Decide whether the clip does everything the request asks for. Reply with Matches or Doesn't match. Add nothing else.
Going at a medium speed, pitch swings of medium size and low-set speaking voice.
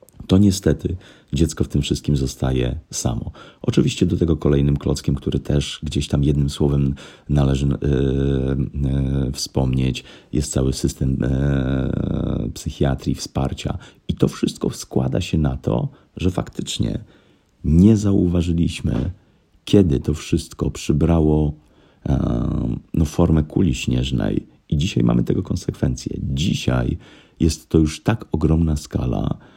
Matches